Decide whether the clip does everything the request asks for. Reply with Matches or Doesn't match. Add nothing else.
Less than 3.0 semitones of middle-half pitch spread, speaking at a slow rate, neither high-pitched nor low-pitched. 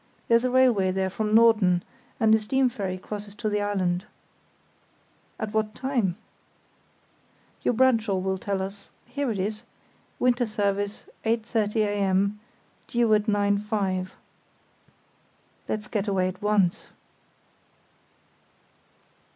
Doesn't match